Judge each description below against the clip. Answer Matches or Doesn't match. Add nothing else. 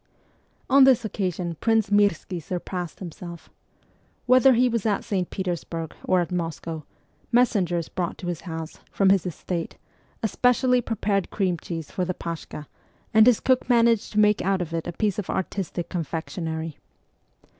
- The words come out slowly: Doesn't match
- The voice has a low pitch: Doesn't match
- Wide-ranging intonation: Doesn't match